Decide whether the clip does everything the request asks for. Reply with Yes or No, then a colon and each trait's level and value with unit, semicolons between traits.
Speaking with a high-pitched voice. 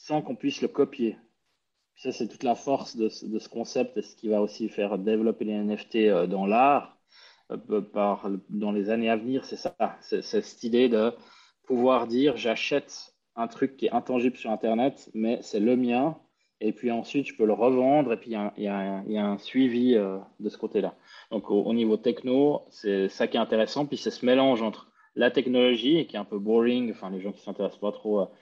No: low, 115 Hz